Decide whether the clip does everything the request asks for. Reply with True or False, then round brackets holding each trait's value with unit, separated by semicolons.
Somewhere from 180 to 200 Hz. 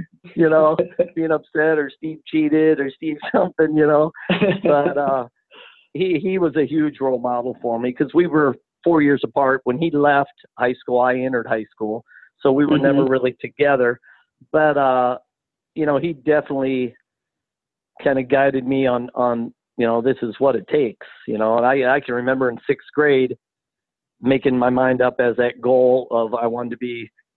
False (135 Hz)